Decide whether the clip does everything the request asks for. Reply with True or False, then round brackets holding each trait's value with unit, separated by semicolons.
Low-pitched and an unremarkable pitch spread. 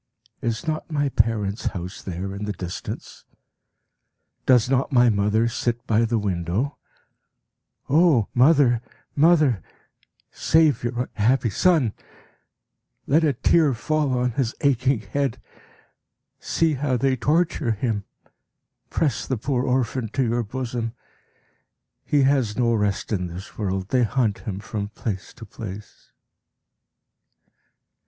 True (120 Hz; 4.5 semitones)